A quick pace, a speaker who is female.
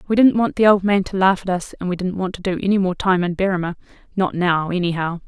Yes: fast, 260 wpm; female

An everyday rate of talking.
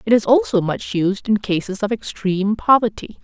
Yes: average, 185 wpm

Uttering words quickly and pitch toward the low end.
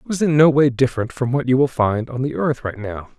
Yes: fast, 300 wpm; low, 130 Hz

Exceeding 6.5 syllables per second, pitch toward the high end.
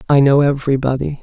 No: 6.7 syllables/s; medium, 140 Hz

